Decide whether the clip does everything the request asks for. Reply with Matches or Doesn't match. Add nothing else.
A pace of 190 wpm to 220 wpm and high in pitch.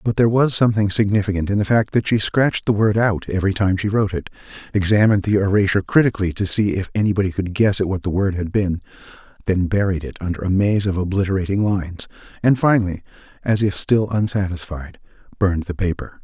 Doesn't match